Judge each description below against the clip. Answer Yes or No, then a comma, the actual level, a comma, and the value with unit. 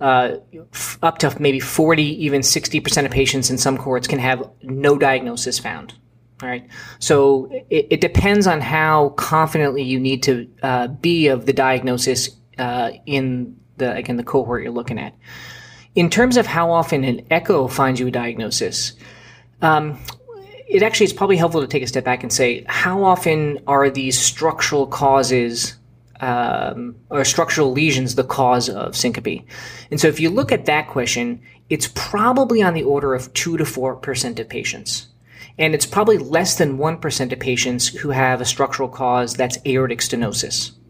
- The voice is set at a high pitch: No, low, 135 Hz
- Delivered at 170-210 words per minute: Yes, average, 175 wpm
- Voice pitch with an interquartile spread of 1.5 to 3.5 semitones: No, average, 3.9 semitones